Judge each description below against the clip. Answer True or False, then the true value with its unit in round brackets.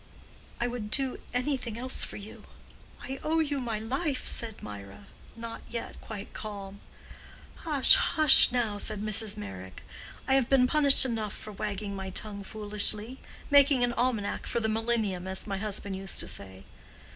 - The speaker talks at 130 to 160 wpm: True (155 wpm)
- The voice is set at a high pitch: True (220 Hz)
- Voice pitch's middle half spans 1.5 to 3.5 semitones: False (4.0 semitones)